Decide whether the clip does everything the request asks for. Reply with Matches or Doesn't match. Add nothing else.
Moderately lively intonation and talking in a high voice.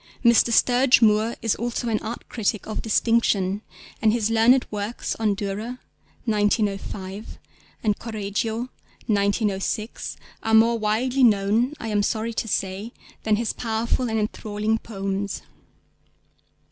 Doesn't match